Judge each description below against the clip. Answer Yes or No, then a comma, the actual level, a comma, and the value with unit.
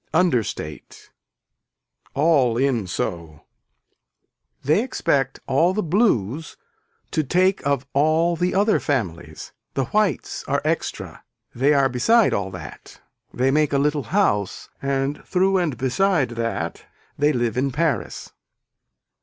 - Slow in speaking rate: Yes, slow, 120 wpm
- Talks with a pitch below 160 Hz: Yes, medium, 140 Hz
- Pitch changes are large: Yes, wide, 6.0 semitones